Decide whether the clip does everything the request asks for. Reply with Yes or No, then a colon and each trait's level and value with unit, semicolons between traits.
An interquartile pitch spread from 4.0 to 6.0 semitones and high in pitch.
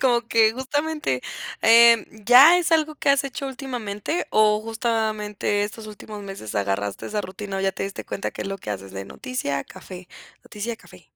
Yes: average, 4.6 semitones; high, 215 Hz